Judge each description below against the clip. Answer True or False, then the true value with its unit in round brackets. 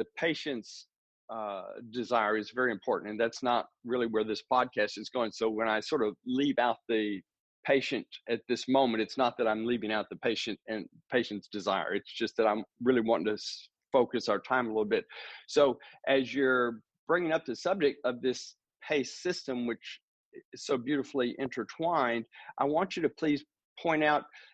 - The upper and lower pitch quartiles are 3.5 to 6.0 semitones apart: True (3.9 semitones)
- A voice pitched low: True (125 Hz)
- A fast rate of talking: False (185 wpm)